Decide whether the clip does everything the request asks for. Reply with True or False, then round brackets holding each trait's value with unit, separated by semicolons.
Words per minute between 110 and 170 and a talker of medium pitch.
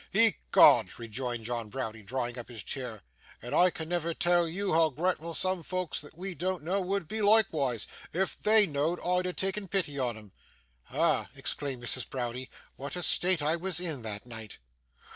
False (180 wpm; 155 Hz)